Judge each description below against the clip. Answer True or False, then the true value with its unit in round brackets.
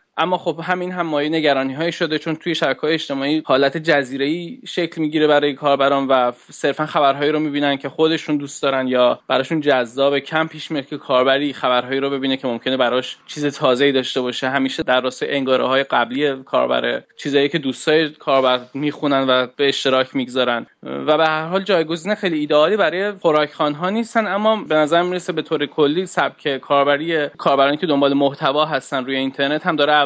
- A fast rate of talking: True (175 wpm)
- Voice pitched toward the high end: False (145 Hz)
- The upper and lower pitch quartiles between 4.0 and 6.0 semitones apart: False (3.0 semitones)